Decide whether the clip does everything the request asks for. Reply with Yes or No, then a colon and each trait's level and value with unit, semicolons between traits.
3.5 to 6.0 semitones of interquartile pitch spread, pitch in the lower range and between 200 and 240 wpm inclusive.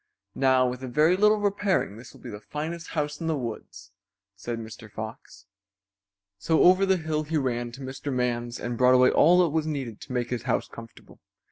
Yes: average, 5.0 semitones; low, 130 Hz; fast, 205 wpm